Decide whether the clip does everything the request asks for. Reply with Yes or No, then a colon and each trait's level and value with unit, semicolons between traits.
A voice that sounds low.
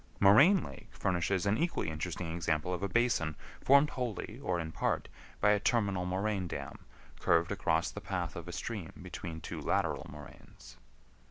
Yes: very low, 95 Hz